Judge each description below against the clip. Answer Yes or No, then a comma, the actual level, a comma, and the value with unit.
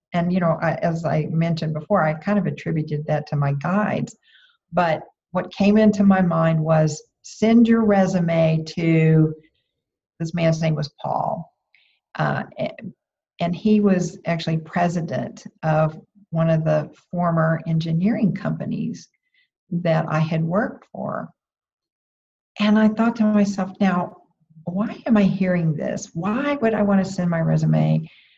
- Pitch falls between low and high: Yes, medium, 175 Hz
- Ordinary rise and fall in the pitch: Yes, average, 4.2 semitones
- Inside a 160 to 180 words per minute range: No, average, 145 wpm